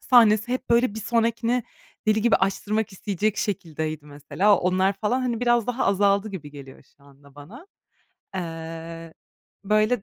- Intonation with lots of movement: Yes, wide, 5.7 semitones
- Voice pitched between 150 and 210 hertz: Yes, high, 200 Hz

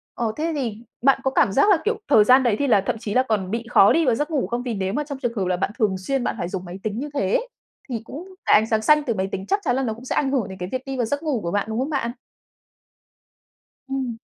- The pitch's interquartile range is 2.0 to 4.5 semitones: No, average, 4.9 semitones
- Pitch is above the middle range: Yes, high, 240 Hz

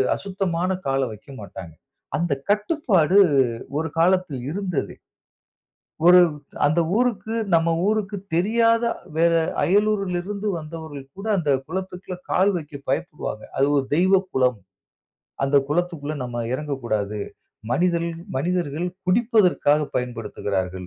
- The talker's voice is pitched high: No, medium, 170 Hz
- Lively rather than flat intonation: Yes, wide, 5.7 semitones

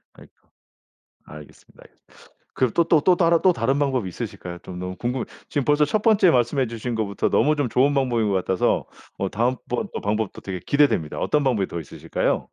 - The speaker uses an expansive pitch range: Yes, wide, 6.3 semitones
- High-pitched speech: No, low, 125 Hz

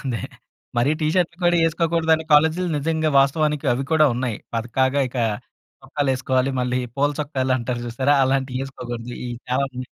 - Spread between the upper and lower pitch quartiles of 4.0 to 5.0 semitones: No, average, 3.4 semitones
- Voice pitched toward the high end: No, low, 135 Hz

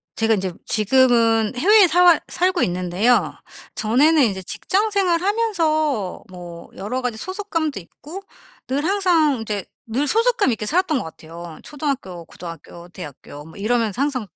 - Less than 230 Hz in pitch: No, very high, 250 Hz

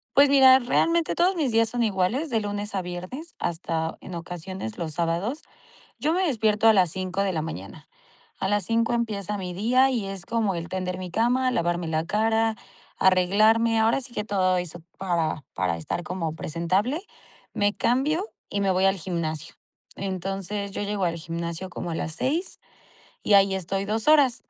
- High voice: Yes, high, 195 Hz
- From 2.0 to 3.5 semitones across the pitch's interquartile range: No, average, 4.6 semitones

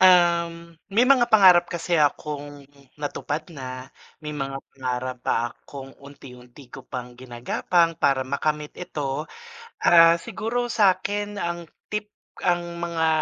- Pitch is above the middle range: No, medium, 160 Hz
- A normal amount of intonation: Yes, average, 4.4 semitones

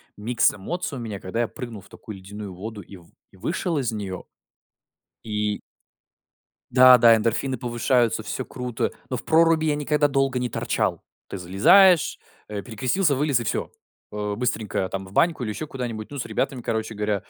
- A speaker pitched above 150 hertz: No, low, 115 Hz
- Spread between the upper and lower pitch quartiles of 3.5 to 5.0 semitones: Yes, average, 4.5 semitones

